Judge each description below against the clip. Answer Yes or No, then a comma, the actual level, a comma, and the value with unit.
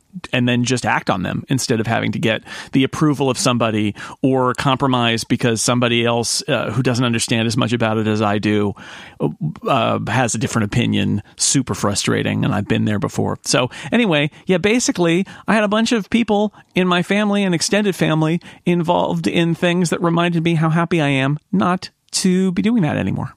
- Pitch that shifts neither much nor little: No, wide, 7.2 semitones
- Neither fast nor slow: Yes, average, 195 wpm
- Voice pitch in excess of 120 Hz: Yes, medium, 140 Hz